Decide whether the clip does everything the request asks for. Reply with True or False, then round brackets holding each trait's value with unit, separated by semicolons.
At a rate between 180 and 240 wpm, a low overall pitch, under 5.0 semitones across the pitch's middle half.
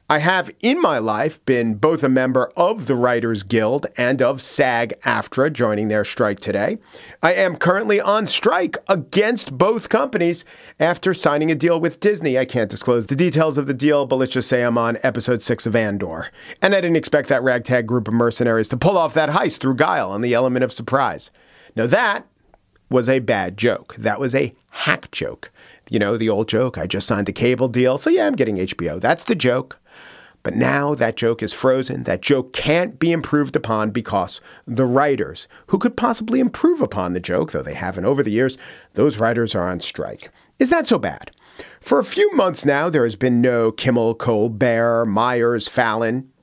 False (200 wpm; 130 Hz; 5.5 semitones)